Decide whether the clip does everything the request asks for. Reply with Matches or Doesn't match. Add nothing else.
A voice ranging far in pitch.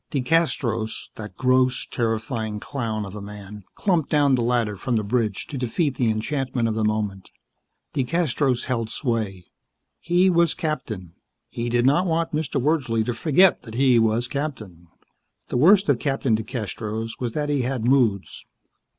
Doesn't match